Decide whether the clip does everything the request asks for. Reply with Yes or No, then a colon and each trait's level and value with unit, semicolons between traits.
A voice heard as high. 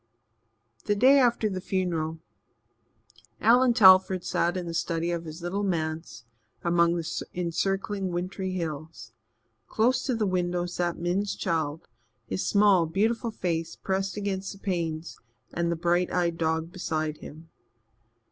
No: medium, 175 Hz